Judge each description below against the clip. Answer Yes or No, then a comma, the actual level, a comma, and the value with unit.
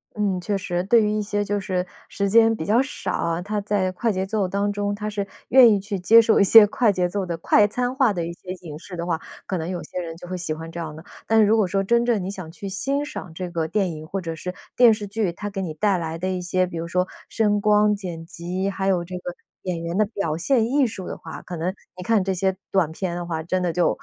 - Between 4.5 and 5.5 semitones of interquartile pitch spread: No, average, 3.2 semitones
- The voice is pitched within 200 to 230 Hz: No, high, 190 Hz